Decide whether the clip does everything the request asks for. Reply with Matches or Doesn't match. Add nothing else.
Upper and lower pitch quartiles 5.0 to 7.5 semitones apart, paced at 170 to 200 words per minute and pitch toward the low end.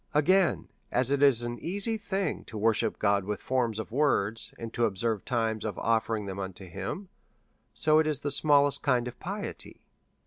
Matches